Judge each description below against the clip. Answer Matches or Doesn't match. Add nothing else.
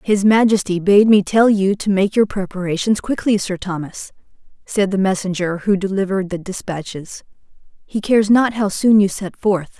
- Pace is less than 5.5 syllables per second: Matches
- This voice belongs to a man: Doesn't match